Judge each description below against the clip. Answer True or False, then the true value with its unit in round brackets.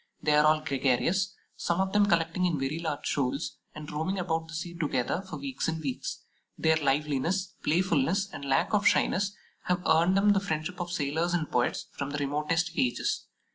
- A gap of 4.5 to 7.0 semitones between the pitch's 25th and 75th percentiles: False (3.7 semitones)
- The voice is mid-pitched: True (160 Hz)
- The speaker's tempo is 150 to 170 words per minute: False (185 wpm)